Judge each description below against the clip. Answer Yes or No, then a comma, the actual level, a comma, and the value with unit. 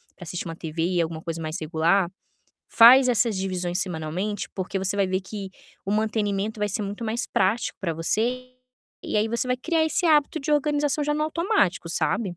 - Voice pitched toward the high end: Yes, high, 205 Hz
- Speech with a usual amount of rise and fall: No, wide, 5.8 semitones